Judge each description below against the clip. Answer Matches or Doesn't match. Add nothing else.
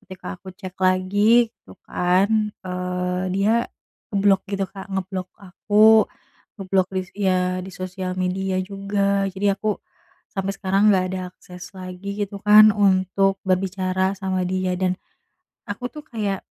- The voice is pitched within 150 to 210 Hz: Matches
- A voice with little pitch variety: Matches